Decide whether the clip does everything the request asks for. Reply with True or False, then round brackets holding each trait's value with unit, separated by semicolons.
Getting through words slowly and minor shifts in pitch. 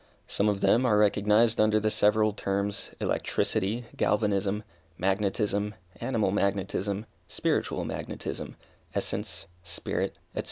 True (110 wpm; 1.4 semitones)